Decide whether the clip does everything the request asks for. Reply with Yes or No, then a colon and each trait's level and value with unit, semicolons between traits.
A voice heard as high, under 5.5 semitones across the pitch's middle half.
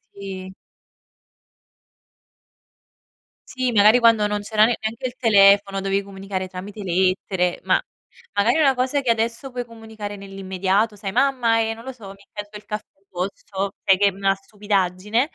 Yes: high, 205 Hz; average, 2.7 semitones